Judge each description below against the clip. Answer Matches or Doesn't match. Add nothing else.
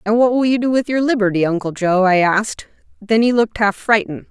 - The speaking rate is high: Matches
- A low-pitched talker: Doesn't match